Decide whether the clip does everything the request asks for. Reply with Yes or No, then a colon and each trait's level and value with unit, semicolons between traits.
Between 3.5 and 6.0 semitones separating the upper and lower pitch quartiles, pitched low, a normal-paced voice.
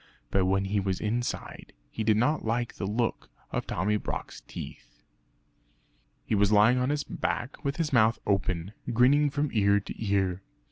Yes: average, 3.9 semitones; low, 110 Hz; average, 170 wpm